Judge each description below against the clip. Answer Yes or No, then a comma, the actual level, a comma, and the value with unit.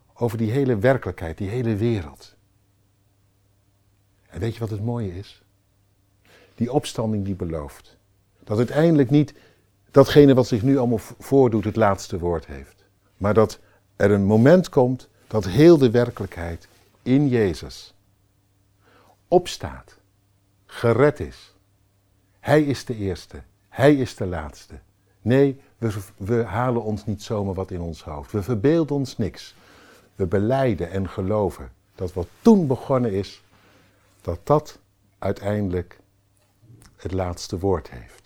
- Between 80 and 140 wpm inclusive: Yes, slow, 135 wpm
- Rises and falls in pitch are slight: No, average, 3.6 semitones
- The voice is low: Yes, low, 100 Hz